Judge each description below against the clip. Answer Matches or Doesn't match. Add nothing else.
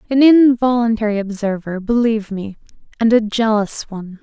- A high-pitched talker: Matches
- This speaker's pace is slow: Matches